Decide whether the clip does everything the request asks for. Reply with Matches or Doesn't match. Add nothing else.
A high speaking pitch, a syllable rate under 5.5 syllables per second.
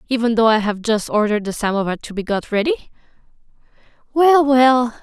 Doesn't match